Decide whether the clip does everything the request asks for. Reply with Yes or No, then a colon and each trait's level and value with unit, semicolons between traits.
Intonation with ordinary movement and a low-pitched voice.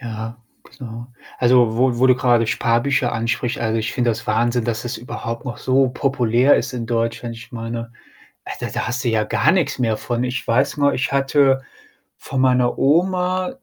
No: narrow, 2.3 semitones; low, 120 Hz